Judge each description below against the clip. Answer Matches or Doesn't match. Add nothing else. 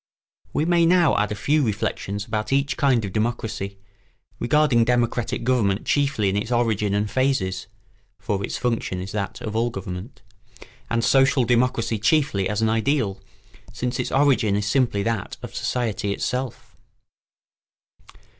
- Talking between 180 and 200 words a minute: Doesn't match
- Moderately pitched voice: Doesn't match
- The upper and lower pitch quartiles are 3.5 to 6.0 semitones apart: Matches